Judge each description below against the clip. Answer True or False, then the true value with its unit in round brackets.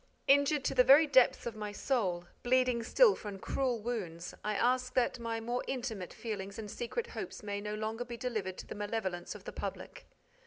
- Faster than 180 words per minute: True (195 wpm)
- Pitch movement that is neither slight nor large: True (3.5 semitones)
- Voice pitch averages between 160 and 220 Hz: False (230 Hz)